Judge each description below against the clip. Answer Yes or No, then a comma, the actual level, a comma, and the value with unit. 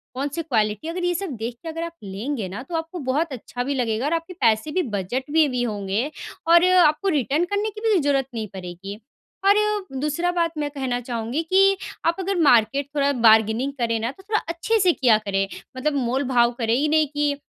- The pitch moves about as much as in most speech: No, wide, 6.3 semitones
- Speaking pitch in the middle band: No, very high, 280 Hz